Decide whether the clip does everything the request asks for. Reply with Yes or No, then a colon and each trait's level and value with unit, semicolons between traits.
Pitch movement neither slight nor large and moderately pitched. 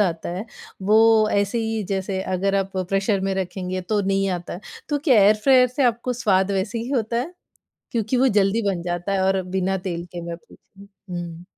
No: average, 3.0 semitones; high, 195 Hz